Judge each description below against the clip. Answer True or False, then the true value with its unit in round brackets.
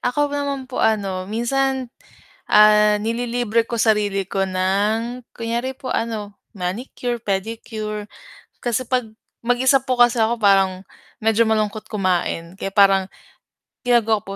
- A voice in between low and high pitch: False (220 Hz)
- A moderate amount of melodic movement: True (3.2 semitones)